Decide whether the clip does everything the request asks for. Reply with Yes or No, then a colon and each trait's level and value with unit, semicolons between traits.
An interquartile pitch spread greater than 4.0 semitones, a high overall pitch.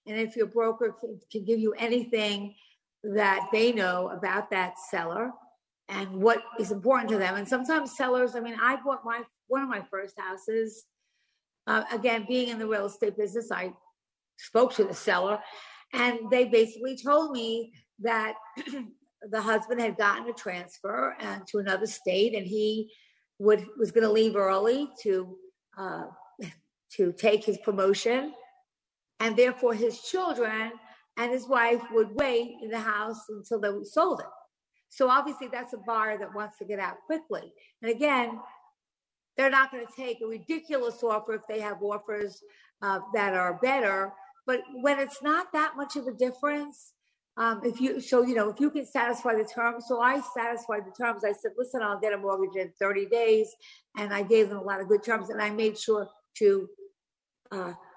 No: average, 3.2 semitones; high, 230 Hz